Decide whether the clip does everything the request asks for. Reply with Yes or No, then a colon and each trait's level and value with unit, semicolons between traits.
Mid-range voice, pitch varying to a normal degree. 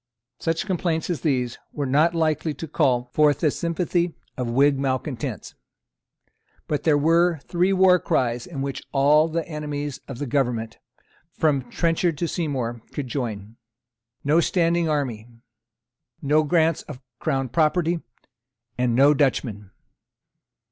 Yes: medium, 145 Hz; average, 4.1 semitones